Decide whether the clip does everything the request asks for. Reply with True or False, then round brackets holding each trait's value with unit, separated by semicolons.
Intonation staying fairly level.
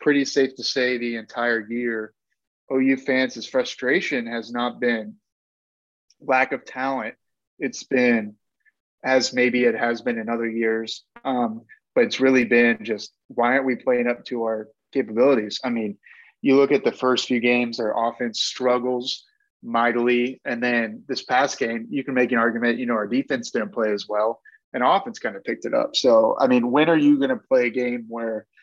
True (2.1 semitones)